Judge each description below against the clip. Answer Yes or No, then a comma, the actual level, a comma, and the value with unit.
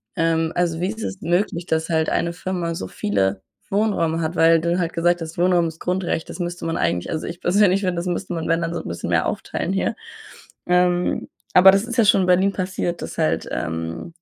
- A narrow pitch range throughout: Yes, narrow, 2.0 semitones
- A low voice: No, medium, 175 Hz